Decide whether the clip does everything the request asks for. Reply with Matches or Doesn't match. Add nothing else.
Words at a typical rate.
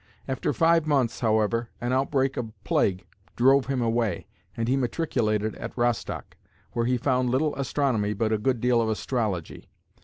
Matches